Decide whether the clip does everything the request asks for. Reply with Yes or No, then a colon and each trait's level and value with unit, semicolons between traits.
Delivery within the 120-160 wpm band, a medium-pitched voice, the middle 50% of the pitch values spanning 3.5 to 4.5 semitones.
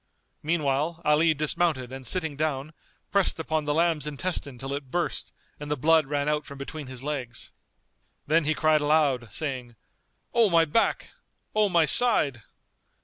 No: average, 155 wpm; medium, 150 Hz; average, 2.8 semitones